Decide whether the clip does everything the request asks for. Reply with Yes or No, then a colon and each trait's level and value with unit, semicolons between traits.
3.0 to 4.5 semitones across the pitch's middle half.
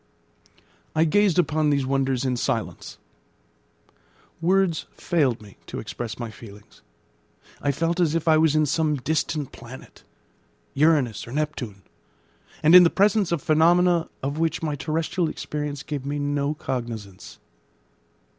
Yes: average, 3.9 semitones